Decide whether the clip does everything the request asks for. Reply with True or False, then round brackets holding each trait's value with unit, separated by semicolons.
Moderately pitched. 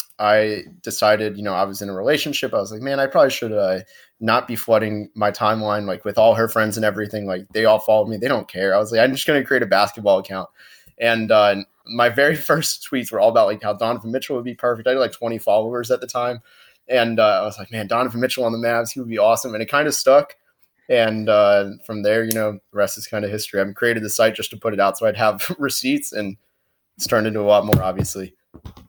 False (110 Hz)